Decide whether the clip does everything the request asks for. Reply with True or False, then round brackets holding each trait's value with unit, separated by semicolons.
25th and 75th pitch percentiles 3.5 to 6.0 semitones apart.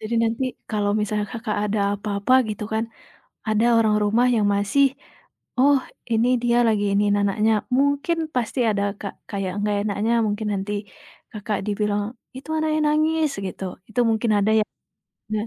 False (2.8 semitones)